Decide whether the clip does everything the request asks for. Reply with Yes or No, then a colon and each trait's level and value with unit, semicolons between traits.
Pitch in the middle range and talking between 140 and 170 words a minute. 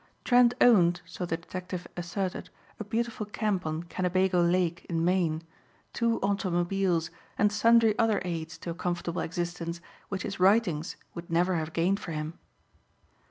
Yes: medium, 180 Hz; average, 150 wpm